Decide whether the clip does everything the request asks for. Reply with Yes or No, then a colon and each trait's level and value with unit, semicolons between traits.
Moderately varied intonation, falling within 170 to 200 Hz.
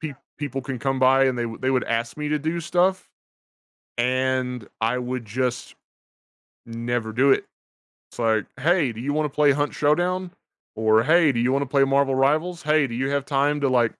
No: average, 3.4 semitones; low, 135 Hz